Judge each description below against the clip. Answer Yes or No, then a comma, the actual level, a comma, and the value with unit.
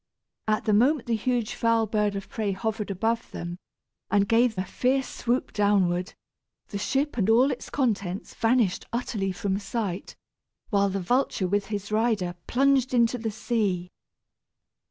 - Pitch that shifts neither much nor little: Yes, average, 3.4 semitones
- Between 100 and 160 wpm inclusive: Yes, average, 155 wpm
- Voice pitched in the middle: No, high, 215 Hz